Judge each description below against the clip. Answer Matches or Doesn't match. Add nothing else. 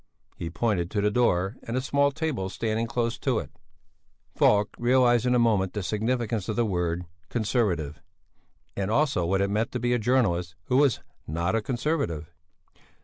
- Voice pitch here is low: Matches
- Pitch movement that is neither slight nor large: Matches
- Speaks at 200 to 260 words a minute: Doesn't match